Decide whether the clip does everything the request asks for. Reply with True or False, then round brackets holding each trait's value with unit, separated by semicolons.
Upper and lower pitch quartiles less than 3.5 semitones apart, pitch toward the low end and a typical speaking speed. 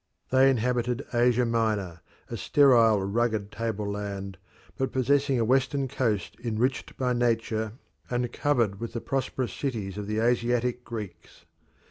False (2.8 semitones; 115 Hz; 130 wpm)